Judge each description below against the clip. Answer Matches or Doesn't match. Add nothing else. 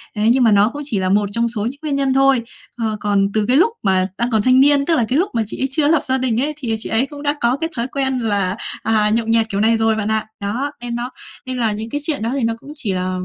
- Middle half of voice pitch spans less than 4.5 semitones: Matches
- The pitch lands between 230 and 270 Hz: Matches